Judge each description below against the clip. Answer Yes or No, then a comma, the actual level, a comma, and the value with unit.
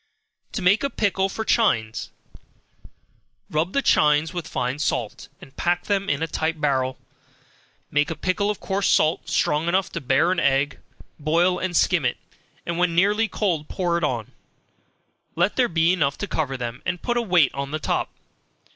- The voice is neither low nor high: Yes, medium, 170 Hz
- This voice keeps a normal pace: Yes, average, 180 wpm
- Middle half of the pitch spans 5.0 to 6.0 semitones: No, average, 4.3 semitones